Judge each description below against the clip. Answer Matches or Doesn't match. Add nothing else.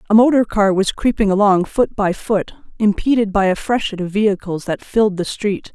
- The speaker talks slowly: Doesn't match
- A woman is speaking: Matches